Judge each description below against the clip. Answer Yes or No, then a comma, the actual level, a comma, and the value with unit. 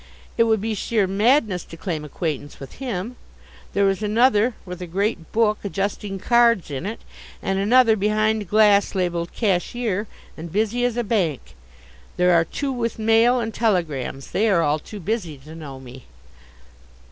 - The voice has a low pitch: No, high, 200 Hz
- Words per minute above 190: No, average, 165 wpm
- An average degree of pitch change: Yes, average, 4.7 semitones